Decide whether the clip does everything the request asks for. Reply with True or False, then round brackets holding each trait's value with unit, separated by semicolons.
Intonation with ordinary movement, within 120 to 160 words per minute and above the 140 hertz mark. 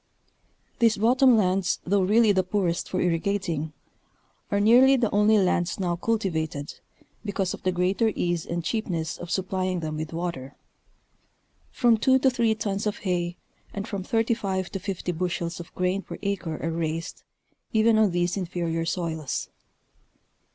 True (3.7 semitones; 150 wpm; 185 Hz)